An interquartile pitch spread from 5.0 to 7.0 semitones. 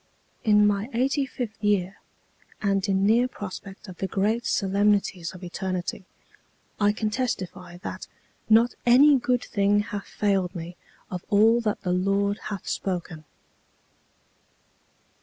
No: average, 2.7 semitones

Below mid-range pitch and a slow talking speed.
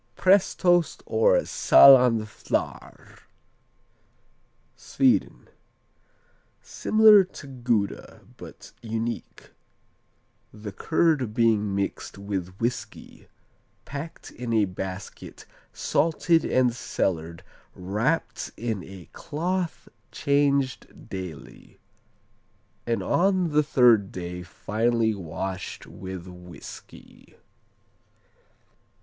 Yes: low, 115 Hz; slow, 80 wpm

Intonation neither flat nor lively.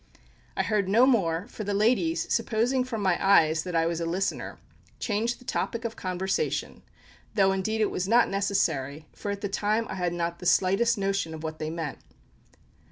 Yes: average, 4.3 semitones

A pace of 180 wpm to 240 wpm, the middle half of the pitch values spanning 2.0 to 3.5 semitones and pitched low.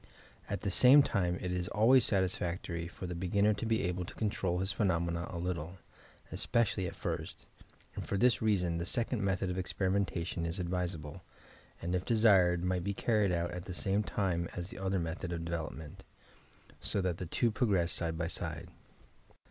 Yes: average, 185 wpm; average, 2.7 semitones; very low, 90 Hz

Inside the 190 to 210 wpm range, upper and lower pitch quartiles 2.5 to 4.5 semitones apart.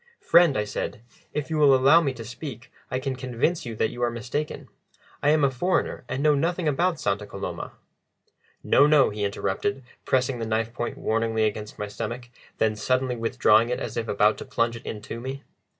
Yes: average, 195 wpm; average, 3.7 semitones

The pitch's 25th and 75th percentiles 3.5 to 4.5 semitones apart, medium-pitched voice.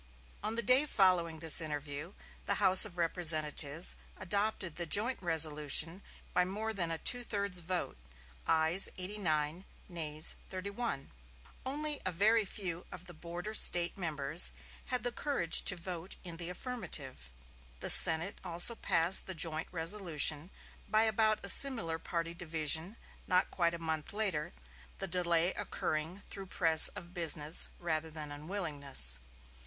Yes: average, 3.8 semitones; medium, 175 Hz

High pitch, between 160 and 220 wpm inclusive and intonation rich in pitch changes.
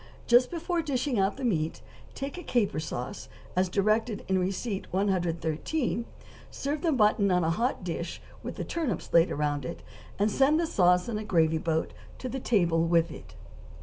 Yes: high, 200 Hz; average, 180 wpm; wide, 6.9 semitones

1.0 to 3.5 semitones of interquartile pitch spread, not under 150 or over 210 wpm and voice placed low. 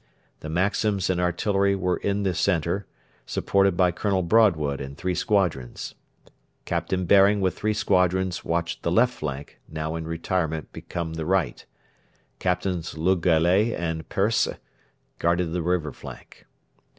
No: average, 3.0 semitones; average, 140 wpm; very low, 90 Hz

